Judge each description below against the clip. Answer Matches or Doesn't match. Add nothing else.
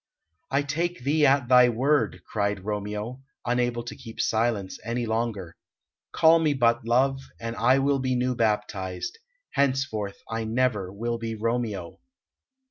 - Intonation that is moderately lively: Matches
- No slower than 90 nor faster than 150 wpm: Matches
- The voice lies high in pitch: Doesn't match